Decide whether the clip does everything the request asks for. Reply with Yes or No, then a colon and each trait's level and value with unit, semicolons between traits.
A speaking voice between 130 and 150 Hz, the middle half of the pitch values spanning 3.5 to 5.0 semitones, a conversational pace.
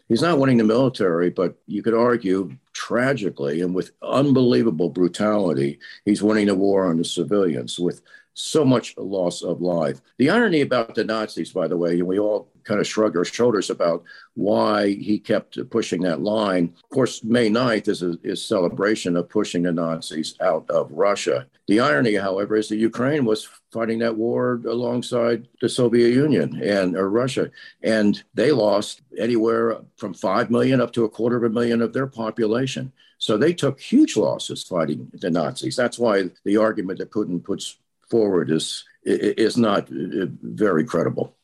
No: low, 110 Hz; average, 4.6 semitones; average, 175 wpm